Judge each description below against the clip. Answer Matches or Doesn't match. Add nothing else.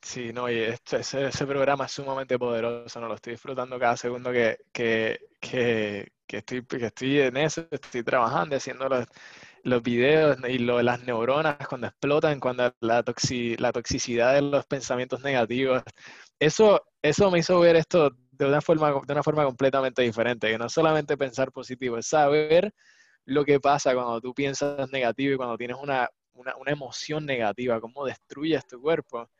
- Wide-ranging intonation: Doesn't match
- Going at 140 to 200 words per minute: Matches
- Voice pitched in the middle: Doesn't match